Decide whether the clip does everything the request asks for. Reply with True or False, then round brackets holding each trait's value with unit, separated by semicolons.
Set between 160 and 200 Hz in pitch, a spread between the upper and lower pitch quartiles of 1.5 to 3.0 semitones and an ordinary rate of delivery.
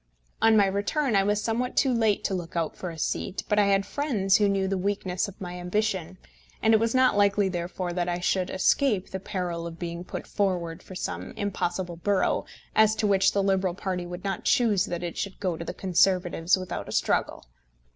False (190 Hz; 2.5 semitones; 215 wpm)